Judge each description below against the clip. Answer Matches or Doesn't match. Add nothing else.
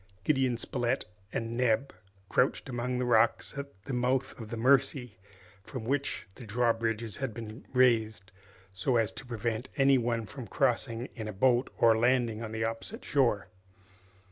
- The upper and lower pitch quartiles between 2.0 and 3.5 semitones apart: Matches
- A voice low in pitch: Matches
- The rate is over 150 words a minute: Matches